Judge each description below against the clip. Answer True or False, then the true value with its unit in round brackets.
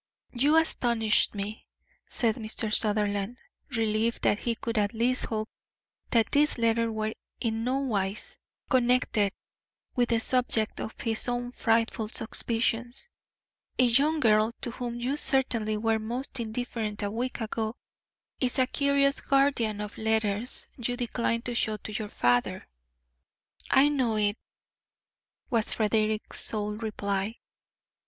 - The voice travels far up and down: False (2.4 semitones)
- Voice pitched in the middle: False (230 Hz)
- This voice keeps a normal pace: False (130 wpm)